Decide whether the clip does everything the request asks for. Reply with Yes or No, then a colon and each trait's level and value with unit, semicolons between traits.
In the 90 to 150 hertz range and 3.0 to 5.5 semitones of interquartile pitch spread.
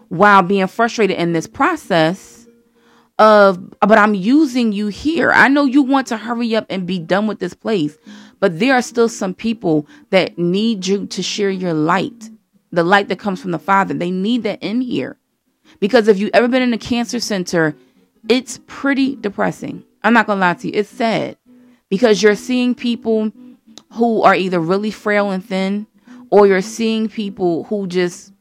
No: high, 210 Hz; average, 3.6 semitones